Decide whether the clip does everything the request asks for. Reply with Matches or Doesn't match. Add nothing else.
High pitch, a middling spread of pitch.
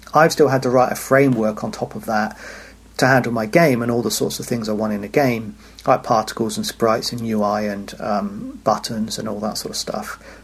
Doesn't match